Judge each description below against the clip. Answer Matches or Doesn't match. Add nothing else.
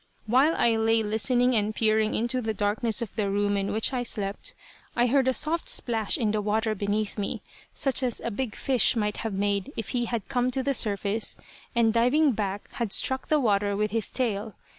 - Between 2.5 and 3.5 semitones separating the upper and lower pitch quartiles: Matches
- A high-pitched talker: Matches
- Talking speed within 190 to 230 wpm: Matches